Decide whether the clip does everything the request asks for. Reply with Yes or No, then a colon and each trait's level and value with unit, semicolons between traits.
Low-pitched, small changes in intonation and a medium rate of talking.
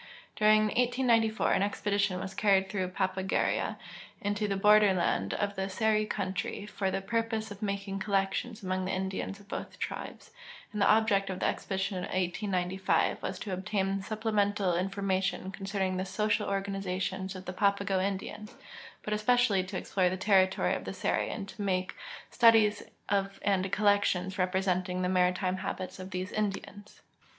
No: high, 195 Hz; narrow, 1.8 semitones; average, 160 wpm